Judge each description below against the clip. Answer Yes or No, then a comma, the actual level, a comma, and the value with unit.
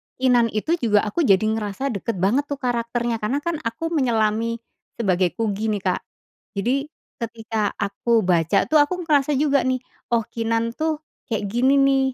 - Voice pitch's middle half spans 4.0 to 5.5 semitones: Yes, average, 4.3 semitones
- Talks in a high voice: Yes, high, 230 Hz